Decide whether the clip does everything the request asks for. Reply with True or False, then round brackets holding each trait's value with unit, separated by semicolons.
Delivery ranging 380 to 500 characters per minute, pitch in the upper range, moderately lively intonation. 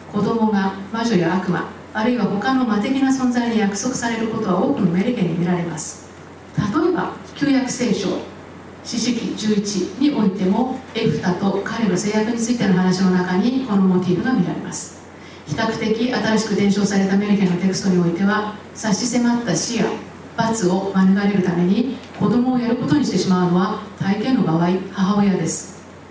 False (360 characters per minute; 205 Hz; 3.7 semitones)